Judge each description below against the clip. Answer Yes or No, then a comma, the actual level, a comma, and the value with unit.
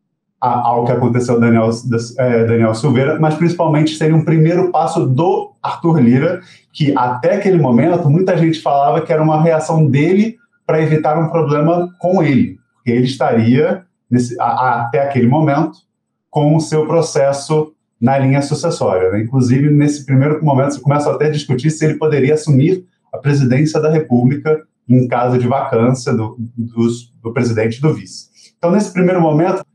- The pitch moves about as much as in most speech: Yes, average, 4.6 semitones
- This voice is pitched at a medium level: Yes, medium, 150 Hz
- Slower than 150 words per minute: No, average, 165 wpm